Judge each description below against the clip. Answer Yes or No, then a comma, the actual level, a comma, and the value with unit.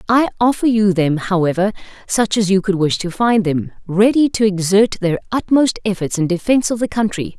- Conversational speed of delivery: Yes, average, 195 wpm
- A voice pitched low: No, high, 200 Hz